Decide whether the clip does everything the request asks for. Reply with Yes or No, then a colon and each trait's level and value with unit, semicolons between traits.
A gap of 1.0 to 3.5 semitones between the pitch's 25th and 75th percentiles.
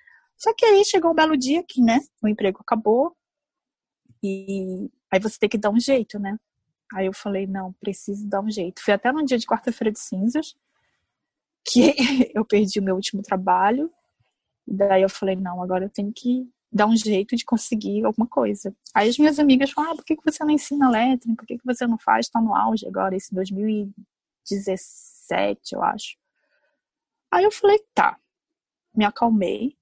No: wide, 5.5 semitones